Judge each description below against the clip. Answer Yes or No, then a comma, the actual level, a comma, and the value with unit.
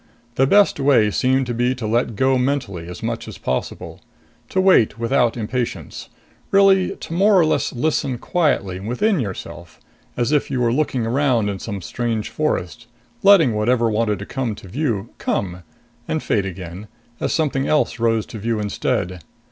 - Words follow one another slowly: No, average, 170 wpm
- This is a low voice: Yes, low, 120 Hz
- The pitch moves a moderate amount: Yes, average, 5.0 semitones